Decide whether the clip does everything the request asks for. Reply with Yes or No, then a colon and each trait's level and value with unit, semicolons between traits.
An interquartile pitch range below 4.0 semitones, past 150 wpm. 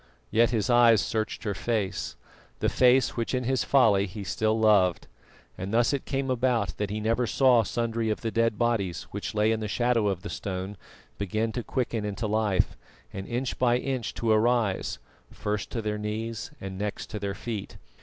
Yes: narrow, 2.5 semitones; average, 190 wpm